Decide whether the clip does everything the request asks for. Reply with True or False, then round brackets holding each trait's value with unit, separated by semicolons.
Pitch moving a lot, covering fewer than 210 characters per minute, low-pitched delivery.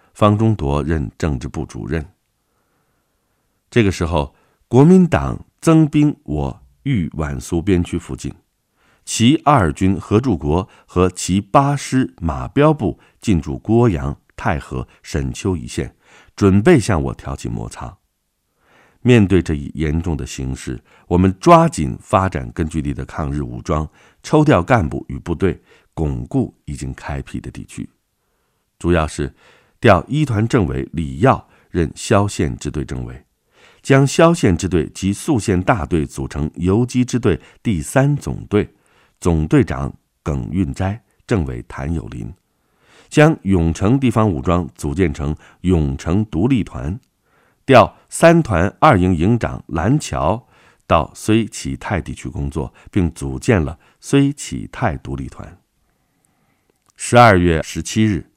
True (7.8 semitones; 195 characters per minute; 90 Hz)